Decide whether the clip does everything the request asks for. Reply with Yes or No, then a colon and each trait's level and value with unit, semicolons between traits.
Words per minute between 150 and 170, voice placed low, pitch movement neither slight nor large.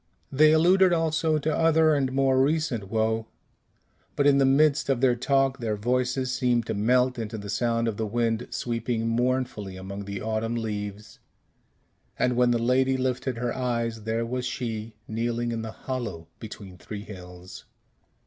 Yes: average, 165 wpm; low, 120 Hz; average, 3.1 semitones